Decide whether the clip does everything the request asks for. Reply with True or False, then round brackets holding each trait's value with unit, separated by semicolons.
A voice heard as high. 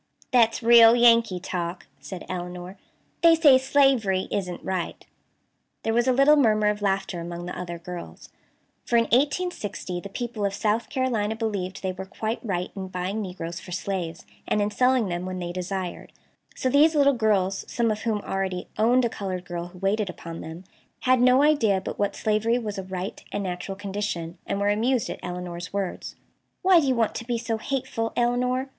True (205 Hz)